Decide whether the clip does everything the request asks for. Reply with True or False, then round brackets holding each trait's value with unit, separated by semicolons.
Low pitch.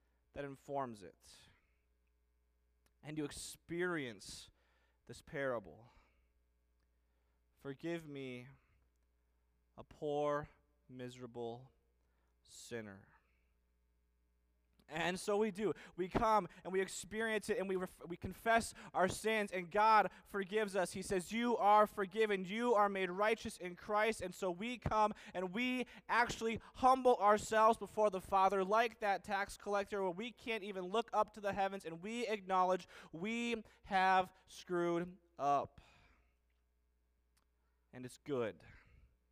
False (180 Hz)